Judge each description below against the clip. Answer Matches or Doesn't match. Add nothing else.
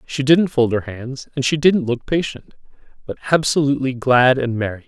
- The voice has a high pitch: Doesn't match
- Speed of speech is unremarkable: Matches